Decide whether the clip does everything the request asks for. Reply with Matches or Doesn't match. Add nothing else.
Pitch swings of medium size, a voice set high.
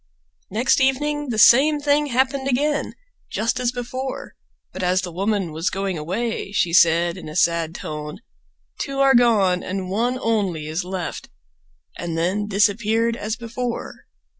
Doesn't match